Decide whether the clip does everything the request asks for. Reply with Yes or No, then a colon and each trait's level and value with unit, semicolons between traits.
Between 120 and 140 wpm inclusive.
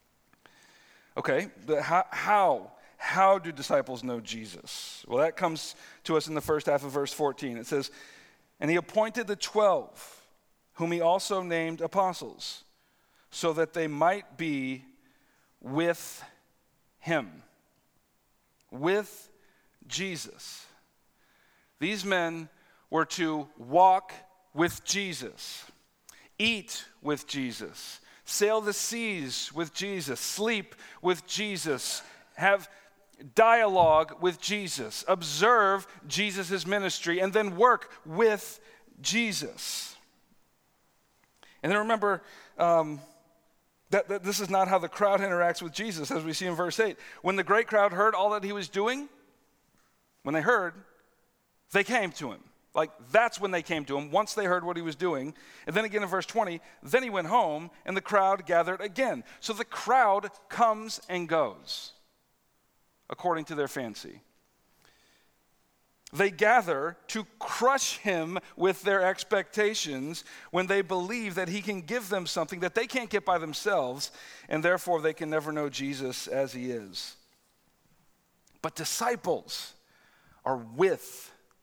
Yes: slow, 135 wpm